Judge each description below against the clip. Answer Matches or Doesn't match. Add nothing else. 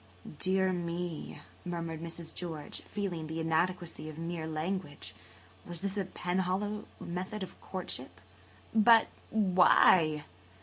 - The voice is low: Doesn't match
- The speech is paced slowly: Matches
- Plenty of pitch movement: Doesn't match